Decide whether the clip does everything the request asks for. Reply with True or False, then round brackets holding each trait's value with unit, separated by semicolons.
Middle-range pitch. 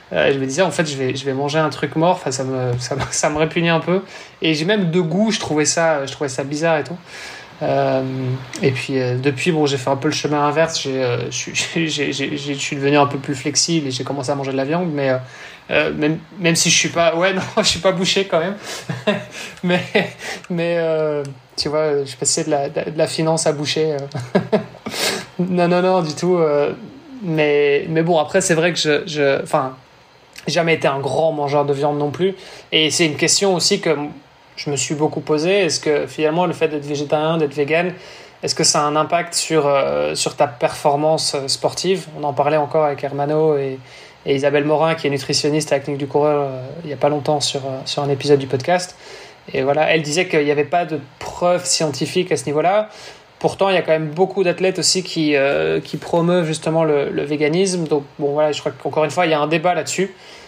True (155 Hz)